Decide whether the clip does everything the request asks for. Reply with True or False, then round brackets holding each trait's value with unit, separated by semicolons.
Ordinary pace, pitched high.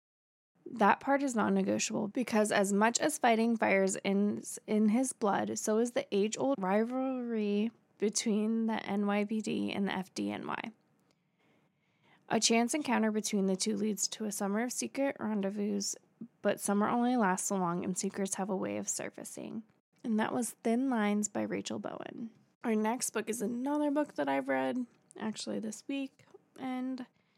True (160 wpm; 215 Hz)